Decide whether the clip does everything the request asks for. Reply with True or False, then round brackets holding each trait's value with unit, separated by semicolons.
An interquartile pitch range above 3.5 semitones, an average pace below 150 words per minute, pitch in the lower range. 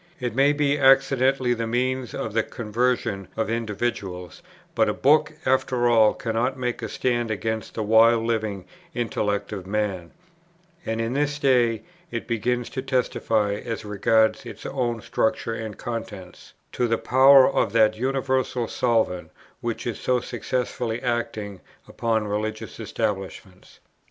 False (2.7 semitones; 140 wpm; 115 Hz)